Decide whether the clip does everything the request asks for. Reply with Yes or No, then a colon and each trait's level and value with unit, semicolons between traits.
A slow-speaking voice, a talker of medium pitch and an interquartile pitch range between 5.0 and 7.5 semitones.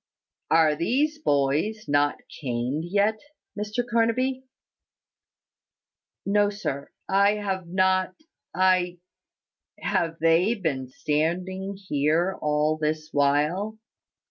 Yes: slow, 95 wpm; medium, 180 Hz; average, 5.3 semitones